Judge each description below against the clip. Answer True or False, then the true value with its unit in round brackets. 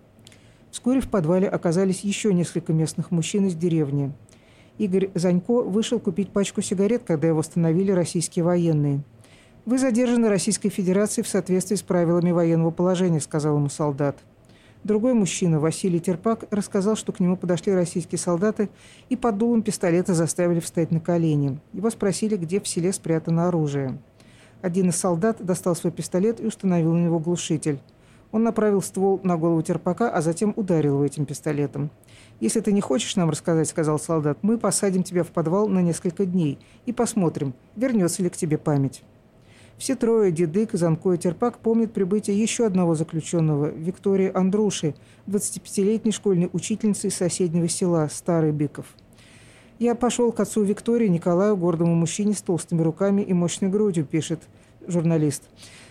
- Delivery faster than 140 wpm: True (155 wpm)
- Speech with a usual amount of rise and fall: True (4.2 semitones)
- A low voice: False (180 Hz)